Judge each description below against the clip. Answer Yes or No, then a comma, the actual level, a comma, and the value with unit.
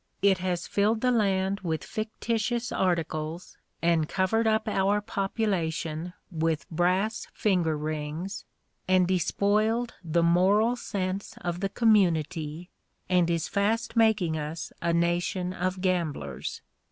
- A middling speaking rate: No, slow, 120 wpm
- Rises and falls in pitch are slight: No, average, 3.7 semitones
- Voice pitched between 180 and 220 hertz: Yes, medium, 185 Hz